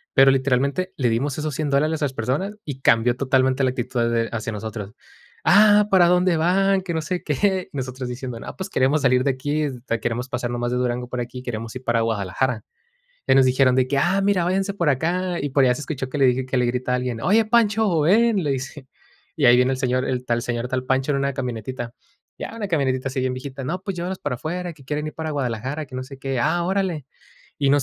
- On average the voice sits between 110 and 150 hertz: Yes, low, 135 Hz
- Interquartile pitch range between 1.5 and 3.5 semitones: No, average, 4.3 semitones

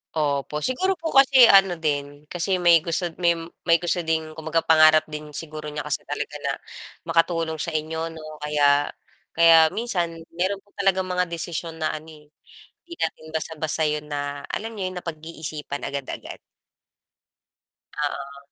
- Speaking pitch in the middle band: Yes, medium, 160 Hz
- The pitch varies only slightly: Yes, narrow, 2.3 semitones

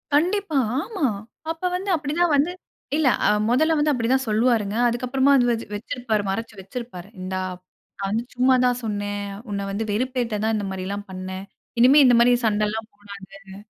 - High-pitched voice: Yes, high, 235 Hz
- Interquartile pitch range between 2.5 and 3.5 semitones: No, average, 4.7 semitones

